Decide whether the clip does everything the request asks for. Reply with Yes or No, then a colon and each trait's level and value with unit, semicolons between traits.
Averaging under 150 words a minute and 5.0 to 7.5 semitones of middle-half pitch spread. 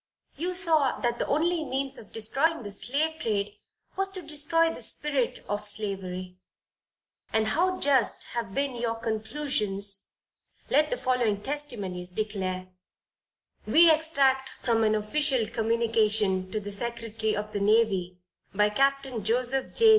Yes: average, 140 wpm; wide, 5.6 semitones